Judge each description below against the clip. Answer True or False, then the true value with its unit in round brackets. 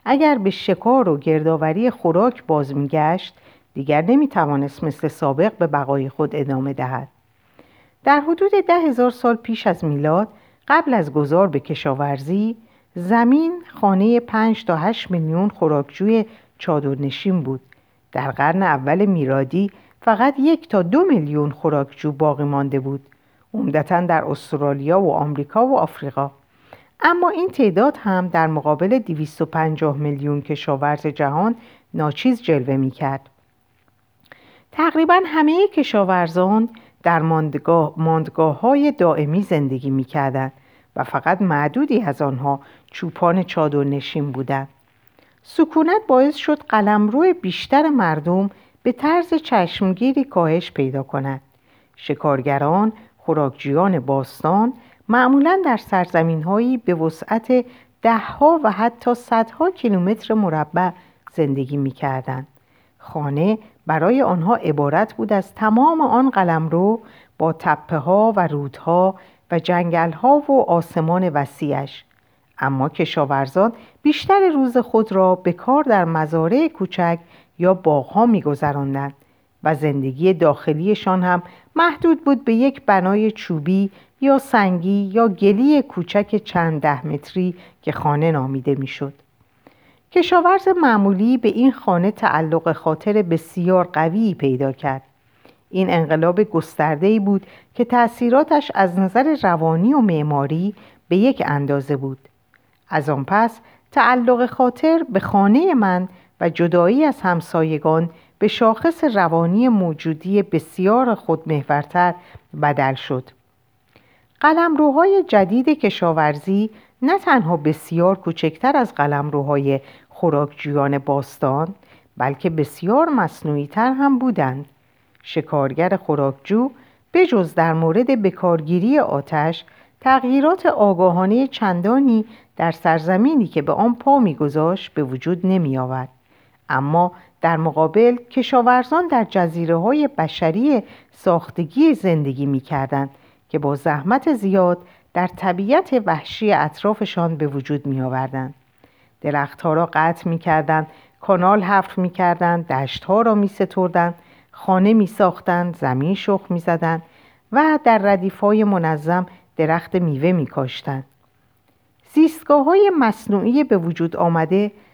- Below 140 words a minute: True (115 wpm)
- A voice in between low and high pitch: True (175 Hz)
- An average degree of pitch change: False (7.4 semitones)